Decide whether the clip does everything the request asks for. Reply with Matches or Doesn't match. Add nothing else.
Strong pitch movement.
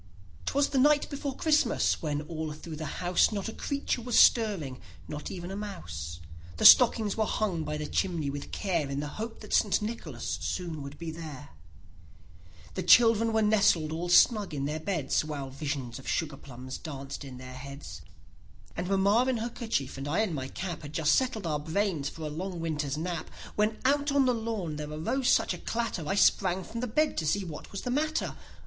Matches